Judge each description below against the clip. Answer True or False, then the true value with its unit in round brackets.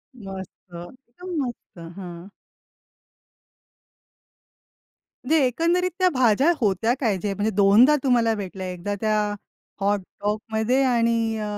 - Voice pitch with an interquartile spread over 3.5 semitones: True (4.3 semitones)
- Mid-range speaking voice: False (220 Hz)